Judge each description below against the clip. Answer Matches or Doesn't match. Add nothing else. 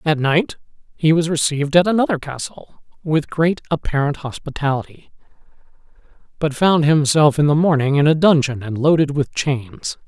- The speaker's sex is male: Matches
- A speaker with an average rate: Matches